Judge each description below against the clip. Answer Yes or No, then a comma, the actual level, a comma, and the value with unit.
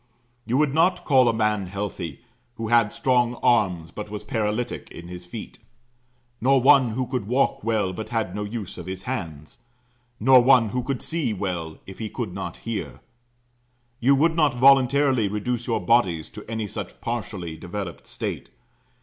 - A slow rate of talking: No, average, 170 wpm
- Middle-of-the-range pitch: No, low, 115 Hz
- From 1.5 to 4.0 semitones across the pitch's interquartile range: No, average, 4.6 semitones